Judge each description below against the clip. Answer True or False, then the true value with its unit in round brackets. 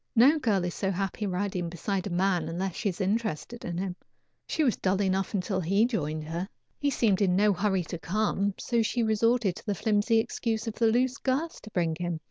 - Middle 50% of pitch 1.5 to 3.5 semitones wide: False (3.9 semitones)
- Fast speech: True (215 wpm)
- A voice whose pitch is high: True (200 Hz)